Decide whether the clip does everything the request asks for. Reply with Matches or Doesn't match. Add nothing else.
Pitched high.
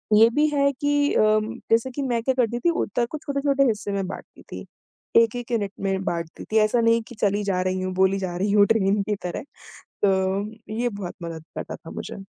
Matches